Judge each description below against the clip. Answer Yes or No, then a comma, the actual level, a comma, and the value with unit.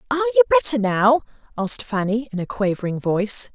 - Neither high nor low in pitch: No, high, 235 Hz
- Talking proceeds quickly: No, average, 170 wpm